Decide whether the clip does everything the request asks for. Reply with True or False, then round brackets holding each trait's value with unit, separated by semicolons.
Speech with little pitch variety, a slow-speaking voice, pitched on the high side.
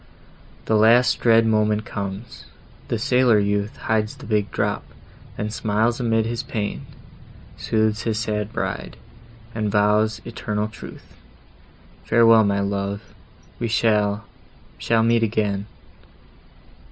False (1.6 semitones; 105 wpm; 110 Hz)